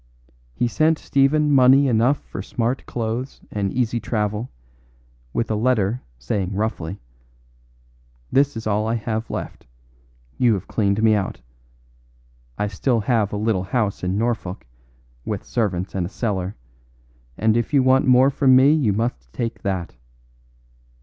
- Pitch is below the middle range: Yes, low, 110 Hz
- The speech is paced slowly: No, average, 145 wpm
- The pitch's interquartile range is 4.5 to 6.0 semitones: No, average, 3.9 semitones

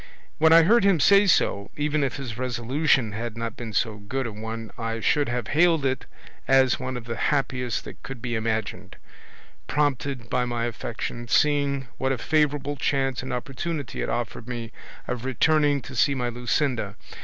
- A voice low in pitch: Yes, low, 130 Hz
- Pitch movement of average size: Yes, average, 3.7 semitones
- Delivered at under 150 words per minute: No, average, 180 wpm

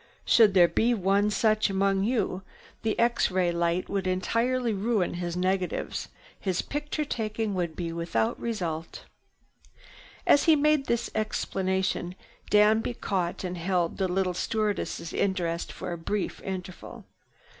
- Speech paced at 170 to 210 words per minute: No, slow, 135 wpm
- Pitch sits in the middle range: No, high, 195 Hz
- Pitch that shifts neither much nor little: Yes, average, 3.5 semitones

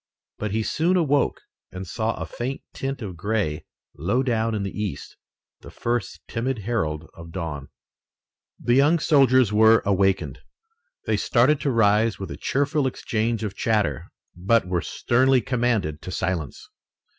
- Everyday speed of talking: Yes, average, 150 wpm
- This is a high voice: No, low, 110 Hz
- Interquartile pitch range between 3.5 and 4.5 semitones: No, average, 5.0 semitones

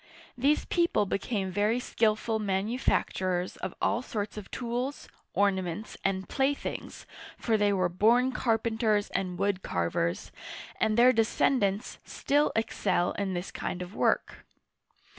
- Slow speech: Yes, slow, 125 wpm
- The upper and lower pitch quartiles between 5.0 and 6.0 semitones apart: No, average, 3.8 semitones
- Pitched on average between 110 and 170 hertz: No, high, 210 Hz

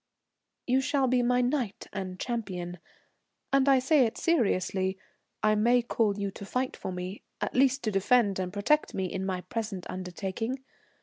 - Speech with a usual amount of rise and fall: Yes, average, 5.0 semitones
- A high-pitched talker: Yes, high, 215 Hz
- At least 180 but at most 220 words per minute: No, average, 170 wpm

